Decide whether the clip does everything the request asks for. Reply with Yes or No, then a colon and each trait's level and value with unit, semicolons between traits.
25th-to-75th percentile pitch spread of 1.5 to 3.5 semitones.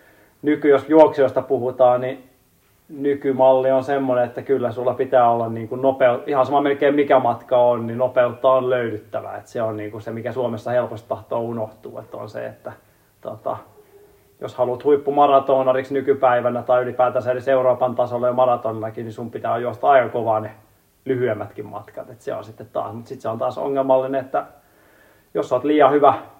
Yes: narrow, 2.6 semitones